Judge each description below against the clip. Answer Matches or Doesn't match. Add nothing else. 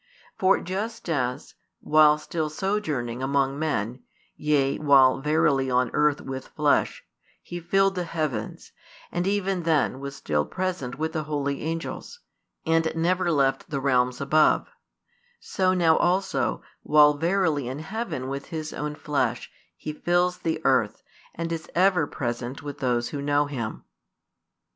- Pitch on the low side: Doesn't match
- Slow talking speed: Doesn't match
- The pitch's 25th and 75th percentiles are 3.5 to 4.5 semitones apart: Matches